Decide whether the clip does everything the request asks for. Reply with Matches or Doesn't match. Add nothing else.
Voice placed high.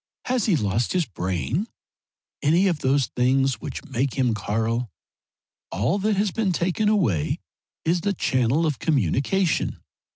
Doesn't match